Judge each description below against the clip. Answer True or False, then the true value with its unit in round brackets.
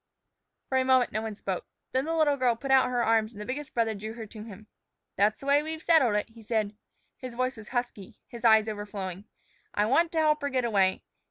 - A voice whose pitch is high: True (235 Hz)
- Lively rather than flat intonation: False (3.8 semitones)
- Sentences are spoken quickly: True (235 wpm)